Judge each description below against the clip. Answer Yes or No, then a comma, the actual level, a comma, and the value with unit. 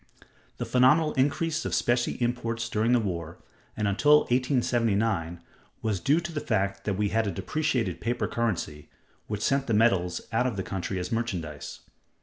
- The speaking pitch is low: Yes, low, 115 Hz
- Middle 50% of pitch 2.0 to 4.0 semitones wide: No, average, 4.5 semitones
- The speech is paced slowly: No, average, 165 wpm